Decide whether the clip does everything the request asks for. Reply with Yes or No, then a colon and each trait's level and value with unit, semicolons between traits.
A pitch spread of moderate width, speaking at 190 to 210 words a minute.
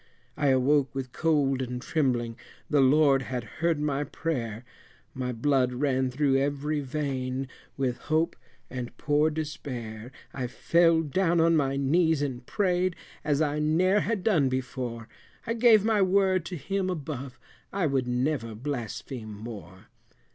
No: average, 4.1 semitones; average, 145 wpm